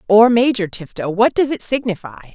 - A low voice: No, high, 220 Hz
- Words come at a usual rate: Yes, average, 155 wpm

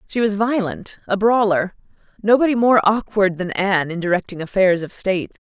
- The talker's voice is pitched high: Yes, high, 200 Hz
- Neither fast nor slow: Yes, average, 165 wpm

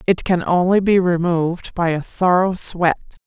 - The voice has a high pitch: No, medium, 175 Hz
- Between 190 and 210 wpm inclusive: No, average, 165 wpm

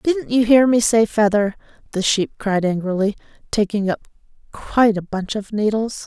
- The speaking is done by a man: No, female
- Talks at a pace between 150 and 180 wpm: Yes, average, 170 wpm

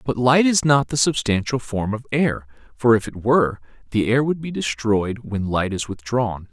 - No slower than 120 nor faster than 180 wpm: No, average, 200 wpm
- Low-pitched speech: Yes, low, 120 Hz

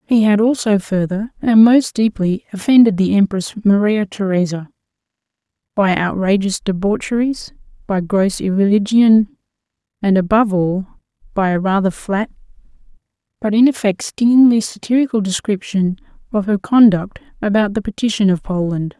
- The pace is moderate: No, slow, 125 wpm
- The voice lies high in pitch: Yes, high, 205 Hz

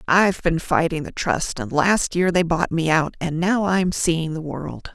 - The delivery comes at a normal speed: No, fast, 220 wpm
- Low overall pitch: No, medium, 170 Hz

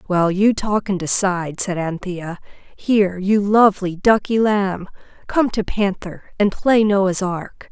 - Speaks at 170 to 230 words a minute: No, average, 150 wpm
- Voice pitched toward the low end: No, high, 195 Hz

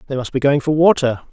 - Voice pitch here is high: No, medium, 140 Hz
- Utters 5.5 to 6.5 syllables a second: Yes, 6.4 syllables/s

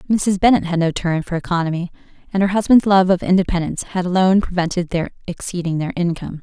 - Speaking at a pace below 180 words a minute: No, average, 185 wpm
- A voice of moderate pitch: Yes, medium, 180 Hz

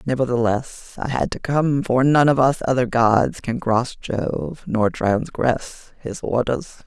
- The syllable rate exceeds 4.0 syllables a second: No, 3.9 syllables/s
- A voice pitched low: Yes, low, 125 Hz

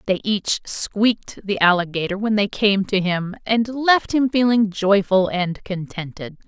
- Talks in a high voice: Yes, high, 205 Hz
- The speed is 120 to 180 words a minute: Yes, average, 160 wpm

